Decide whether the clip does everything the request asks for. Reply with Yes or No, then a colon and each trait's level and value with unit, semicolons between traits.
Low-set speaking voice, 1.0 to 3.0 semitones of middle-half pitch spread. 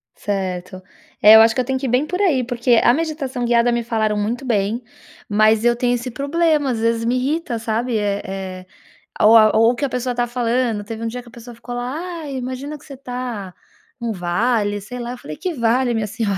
No: high, 235 Hz; average, 2.7 semitones